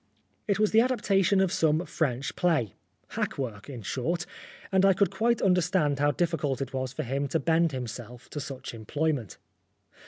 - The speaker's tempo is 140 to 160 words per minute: No, average, 175 wpm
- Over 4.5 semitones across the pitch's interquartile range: Yes, wide, 5.6 semitones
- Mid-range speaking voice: Yes, medium, 155 Hz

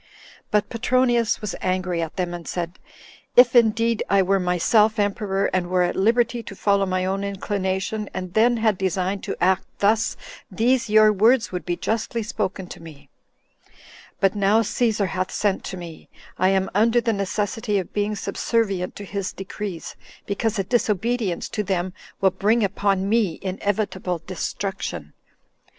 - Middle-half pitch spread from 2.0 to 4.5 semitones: Yes, average, 2.9 semitones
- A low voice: No, high, 200 Hz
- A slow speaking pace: No, average, 160 wpm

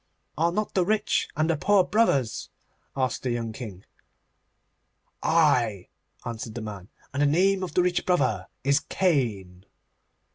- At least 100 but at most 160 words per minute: Yes, average, 145 wpm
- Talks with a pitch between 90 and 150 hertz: Yes, medium, 140 Hz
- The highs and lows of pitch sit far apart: Yes, wide, 8.1 semitones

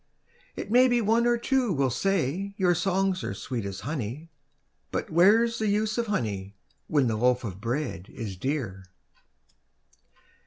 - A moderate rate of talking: Yes, average, 155 wpm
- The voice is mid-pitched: Yes, medium, 160 Hz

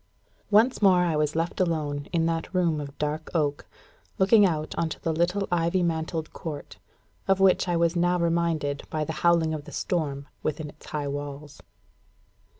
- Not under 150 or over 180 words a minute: Yes, average, 175 wpm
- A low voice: No, medium, 165 Hz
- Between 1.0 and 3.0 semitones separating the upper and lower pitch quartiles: Yes, average, 2.7 semitones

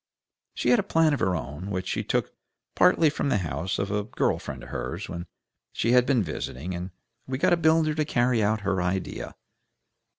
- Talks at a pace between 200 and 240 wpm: Yes, fast, 205 wpm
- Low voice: Yes, low, 105 Hz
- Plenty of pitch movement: Yes, wide, 8.1 semitones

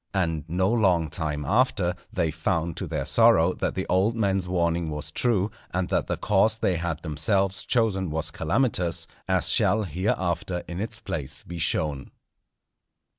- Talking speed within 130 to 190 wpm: Yes, average, 160 wpm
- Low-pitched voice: Yes, very low, 90 Hz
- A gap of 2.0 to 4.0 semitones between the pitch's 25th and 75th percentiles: Yes, average, 3.3 semitones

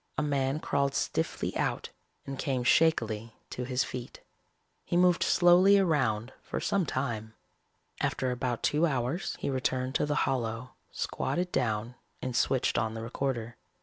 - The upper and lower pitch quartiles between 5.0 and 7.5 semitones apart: No, average, 3.9 semitones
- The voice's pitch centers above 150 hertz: No, low, 130 Hz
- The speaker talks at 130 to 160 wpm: Yes, average, 150 wpm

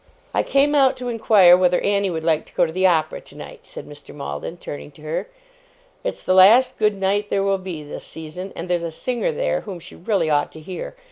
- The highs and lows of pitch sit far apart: No, average, 4.9 semitones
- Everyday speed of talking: No, fast, 225 wpm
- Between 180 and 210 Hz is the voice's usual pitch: Yes, medium, 185 Hz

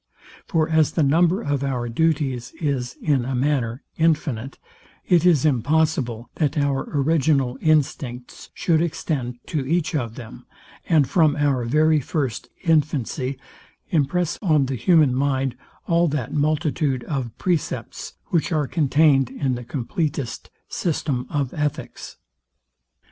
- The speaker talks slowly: Yes, slow, 130 wpm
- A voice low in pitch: No, medium, 145 Hz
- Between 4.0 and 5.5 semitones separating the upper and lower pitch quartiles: No, average, 3.5 semitones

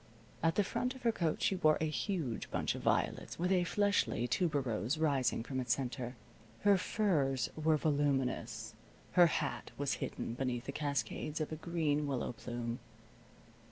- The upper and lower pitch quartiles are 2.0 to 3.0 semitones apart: No, average, 5.0 semitones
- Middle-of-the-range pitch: Yes, medium, 145 Hz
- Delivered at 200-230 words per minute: No, average, 160 wpm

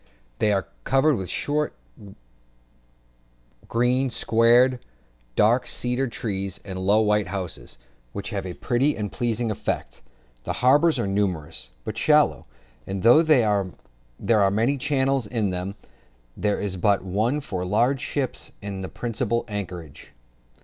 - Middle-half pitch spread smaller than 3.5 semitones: No, average, 4.3 semitones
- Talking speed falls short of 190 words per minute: Yes, slow, 135 wpm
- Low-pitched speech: Yes, low, 105 Hz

